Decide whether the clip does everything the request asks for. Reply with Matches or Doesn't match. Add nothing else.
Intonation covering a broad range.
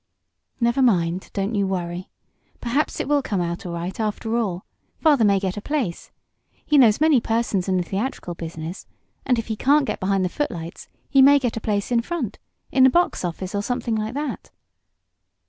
Matches